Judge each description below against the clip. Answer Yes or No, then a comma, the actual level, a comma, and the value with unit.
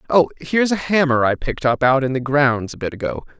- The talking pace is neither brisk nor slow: No, fast, 245 wpm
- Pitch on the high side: No, medium, 140 Hz